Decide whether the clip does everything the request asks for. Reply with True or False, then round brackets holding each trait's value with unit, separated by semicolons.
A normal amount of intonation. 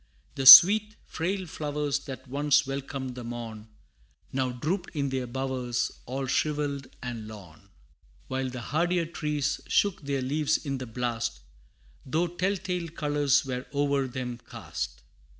True (3.3 semitones)